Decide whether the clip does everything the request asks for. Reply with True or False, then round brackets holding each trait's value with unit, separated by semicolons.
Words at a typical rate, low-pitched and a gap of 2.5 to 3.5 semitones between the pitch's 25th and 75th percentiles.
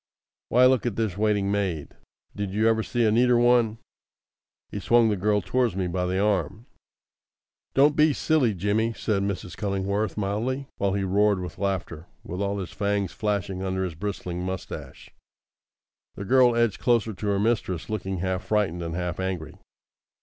True (170 wpm; 100 Hz; 3.1 semitones)